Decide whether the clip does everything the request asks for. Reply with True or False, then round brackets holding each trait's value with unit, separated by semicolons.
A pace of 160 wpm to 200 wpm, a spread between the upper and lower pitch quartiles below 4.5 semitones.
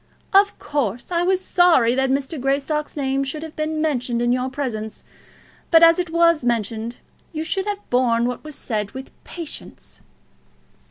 False (165 wpm; 5.0 semitones)